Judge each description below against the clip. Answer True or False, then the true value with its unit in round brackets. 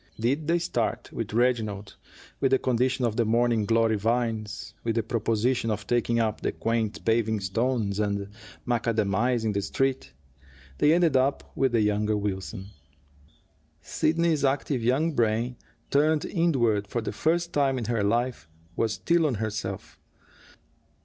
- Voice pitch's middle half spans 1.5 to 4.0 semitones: True (3.4 semitones)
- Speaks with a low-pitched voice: True (115 Hz)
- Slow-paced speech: False (145 wpm)